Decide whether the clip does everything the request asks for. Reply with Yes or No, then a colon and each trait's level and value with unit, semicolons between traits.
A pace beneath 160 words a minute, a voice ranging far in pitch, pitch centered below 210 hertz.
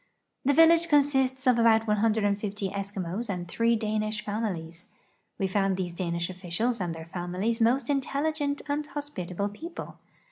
No: average, 140 wpm; wide, 6.0 semitones; high, 215 Hz